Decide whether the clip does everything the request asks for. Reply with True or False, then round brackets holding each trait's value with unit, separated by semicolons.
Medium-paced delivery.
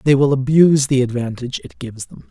False (210 wpm)